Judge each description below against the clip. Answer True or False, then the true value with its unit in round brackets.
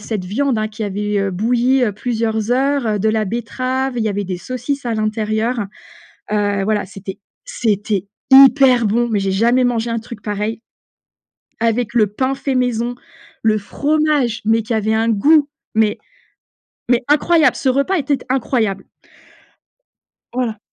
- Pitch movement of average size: True (3.3 semitones)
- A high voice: True (230 Hz)